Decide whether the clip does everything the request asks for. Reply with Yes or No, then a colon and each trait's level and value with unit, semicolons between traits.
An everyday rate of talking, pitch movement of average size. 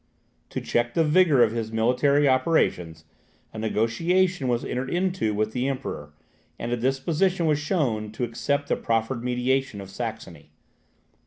Yes: average, 150 wpm; average, 4.8 semitones